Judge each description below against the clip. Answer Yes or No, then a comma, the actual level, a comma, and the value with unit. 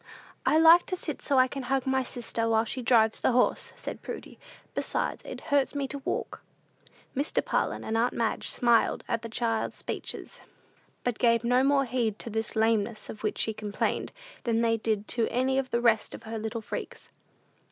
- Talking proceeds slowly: No, average, 195 wpm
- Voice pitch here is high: Yes, high, 235 Hz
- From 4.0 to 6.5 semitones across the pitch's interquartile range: No, average, 2.8 semitones